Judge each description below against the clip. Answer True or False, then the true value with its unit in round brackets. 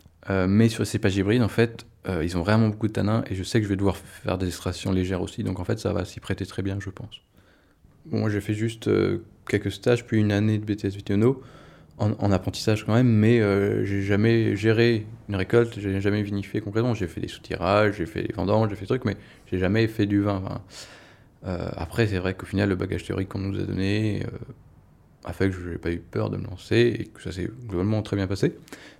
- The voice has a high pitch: False (100 Hz)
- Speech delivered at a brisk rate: True (250 wpm)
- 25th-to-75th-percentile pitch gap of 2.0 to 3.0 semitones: True (2.7 semitones)